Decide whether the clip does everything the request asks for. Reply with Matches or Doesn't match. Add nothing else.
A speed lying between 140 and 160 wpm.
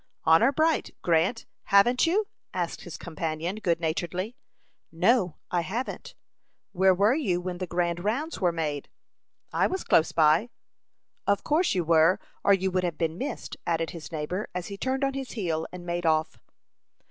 Doesn't match